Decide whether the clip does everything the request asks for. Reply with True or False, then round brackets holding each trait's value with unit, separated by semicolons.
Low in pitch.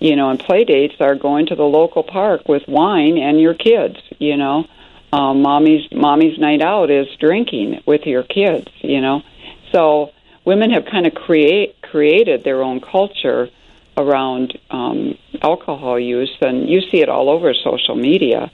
False (150 Hz)